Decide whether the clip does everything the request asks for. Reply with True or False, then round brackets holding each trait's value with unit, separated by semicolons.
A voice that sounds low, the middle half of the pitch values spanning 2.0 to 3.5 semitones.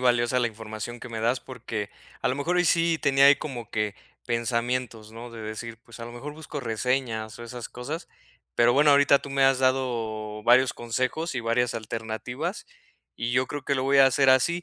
True (125 Hz; 2.9 semitones)